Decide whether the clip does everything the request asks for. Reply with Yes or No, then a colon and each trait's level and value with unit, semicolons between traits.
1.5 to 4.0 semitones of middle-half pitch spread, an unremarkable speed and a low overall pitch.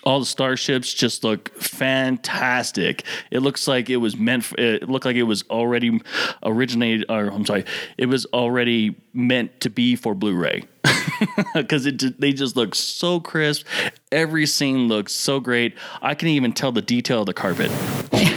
Yes: average, 3.0 semitones; average, 175 wpm; low, 125 Hz